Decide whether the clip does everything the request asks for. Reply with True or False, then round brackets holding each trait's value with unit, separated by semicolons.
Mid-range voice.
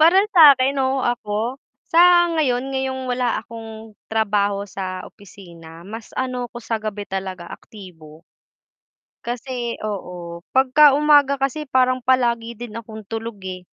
False (235 Hz)